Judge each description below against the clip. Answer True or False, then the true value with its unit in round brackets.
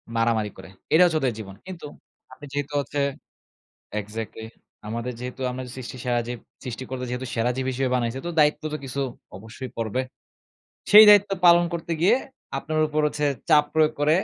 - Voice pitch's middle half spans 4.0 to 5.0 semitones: True (4.5 semitones)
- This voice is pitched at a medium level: False (130 Hz)